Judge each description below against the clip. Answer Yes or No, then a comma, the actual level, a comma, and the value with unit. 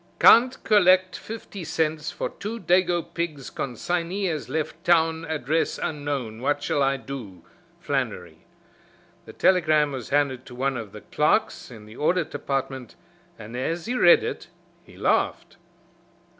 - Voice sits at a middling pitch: Yes, medium, 155 Hz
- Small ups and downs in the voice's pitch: No, average, 4.6 semitones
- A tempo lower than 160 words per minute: Yes, average, 145 wpm